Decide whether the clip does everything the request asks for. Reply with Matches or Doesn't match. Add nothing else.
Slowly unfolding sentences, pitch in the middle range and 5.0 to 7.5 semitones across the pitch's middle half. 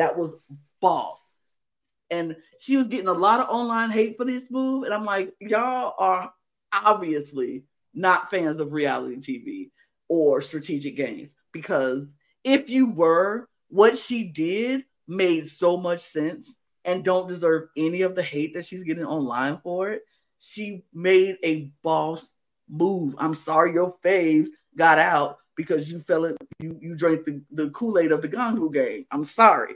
Doesn't match